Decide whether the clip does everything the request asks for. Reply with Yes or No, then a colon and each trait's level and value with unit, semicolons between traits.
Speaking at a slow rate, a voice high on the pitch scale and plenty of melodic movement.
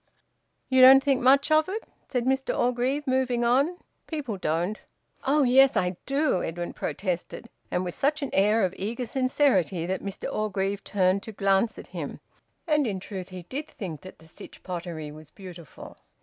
No: average, 175 wpm; high, 220 Hz; wide, 6.4 semitones